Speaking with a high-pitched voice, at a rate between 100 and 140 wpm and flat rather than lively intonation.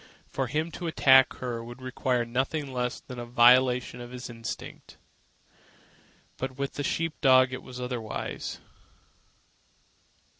No: low, 125 Hz; slow, 135 wpm; narrow, 1.5 semitones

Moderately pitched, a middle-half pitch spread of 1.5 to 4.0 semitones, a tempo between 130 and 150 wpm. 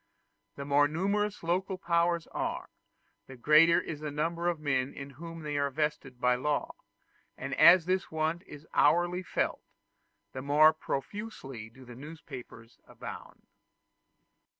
Yes: medium, 155 Hz; average, 3.4 semitones; slow, 135 wpm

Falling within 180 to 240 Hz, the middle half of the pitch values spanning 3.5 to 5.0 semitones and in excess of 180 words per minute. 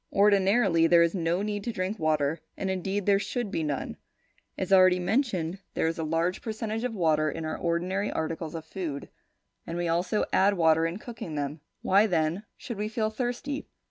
Yes: medium, 185 Hz; average, 4.1 semitones; average, 190 wpm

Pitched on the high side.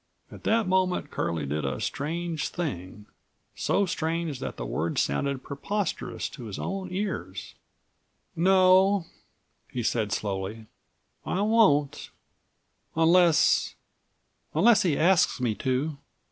No: medium, 155 Hz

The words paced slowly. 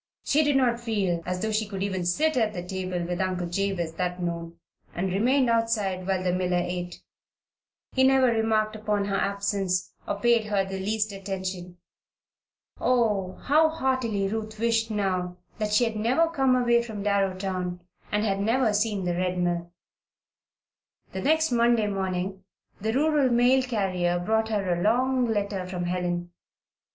No: average, 165 wpm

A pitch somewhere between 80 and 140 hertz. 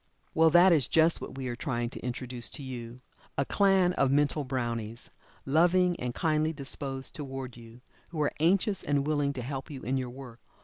Yes: low, 135 Hz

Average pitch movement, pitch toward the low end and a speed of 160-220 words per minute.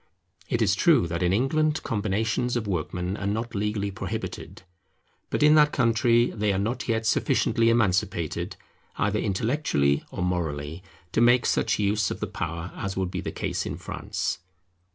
Yes: average, 4.2 semitones; low, 105 Hz; average, 165 wpm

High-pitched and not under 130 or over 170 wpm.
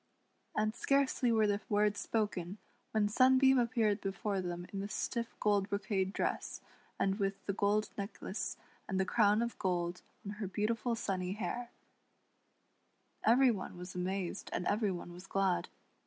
Yes: high, 205 Hz; average, 155 wpm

